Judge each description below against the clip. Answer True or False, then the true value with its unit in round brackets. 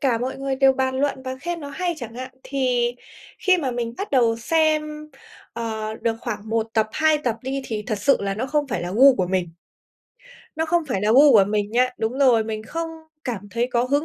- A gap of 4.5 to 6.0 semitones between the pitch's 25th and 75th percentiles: False (4.1 semitones)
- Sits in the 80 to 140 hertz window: False (255 Hz)